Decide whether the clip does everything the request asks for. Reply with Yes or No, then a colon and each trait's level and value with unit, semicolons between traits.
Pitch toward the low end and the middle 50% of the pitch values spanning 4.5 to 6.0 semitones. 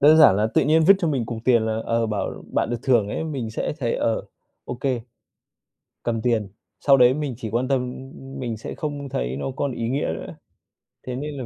No: low, 125 Hz; average, 3.5 semitones